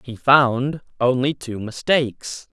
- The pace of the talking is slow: Yes, slow, 115 wpm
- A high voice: No, low, 130 Hz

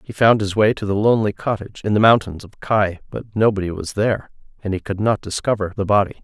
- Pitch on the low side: Yes, low, 100 Hz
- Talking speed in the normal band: No, fast, 230 wpm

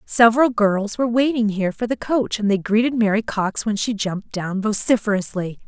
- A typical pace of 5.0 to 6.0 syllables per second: Yes, 5.4 syllables/s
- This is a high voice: Yes, high, 215 Hz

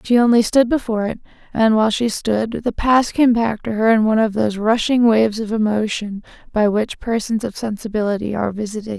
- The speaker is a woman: Yes, female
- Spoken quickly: Yes, fast, 220 wpm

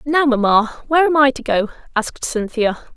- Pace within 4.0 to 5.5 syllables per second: Yes, 5.4 syllables/s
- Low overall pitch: No, very high, 255 Hz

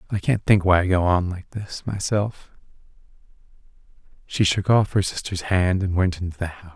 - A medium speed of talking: Yes, average, 185 wpm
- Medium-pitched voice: No, very low, 95 Hz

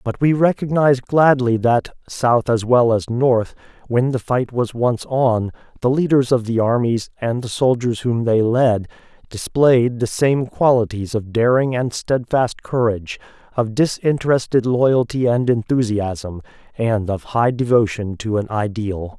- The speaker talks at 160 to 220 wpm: No, average, 150 wpm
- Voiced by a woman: No, male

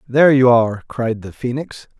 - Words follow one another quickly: No, average, 180 wpm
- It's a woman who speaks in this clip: No, male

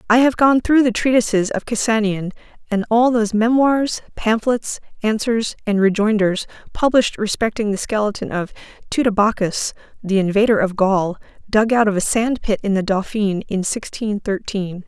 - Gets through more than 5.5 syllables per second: No, 5.0 syllables/s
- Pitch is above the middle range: Yes, high, 215 Hz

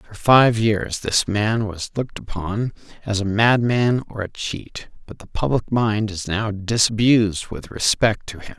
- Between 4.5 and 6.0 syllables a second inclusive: No, 4.1 syllables/s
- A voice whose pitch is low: Yes, low, 105 Hz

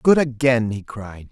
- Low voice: Yes, low, 120 Hz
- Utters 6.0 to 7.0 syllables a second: No, 4.1 syllables/s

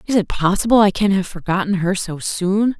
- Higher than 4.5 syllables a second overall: Yes, 5.3 syllables/s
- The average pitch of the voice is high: Yes, high, 195 Hz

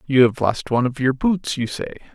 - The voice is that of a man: Yes, male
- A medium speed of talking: No, fast, 250 wpm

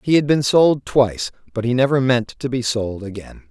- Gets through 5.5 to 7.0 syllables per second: No, 5.1 syllables/s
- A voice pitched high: No, low, 125 Hz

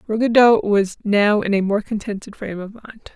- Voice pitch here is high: Yes, high, 215 Hz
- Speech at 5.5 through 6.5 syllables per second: No, 5.2 syllables/s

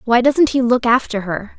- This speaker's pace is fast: Yes, fast, 225 wpm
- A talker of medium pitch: No, high, 240 Hz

